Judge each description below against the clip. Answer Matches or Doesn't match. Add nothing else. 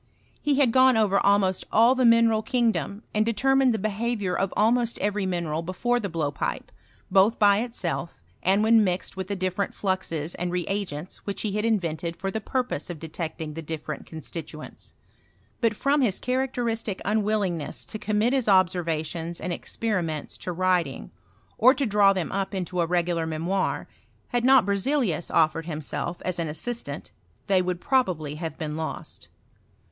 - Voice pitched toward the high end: Matches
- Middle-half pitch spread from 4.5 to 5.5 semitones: Matches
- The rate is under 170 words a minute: Matches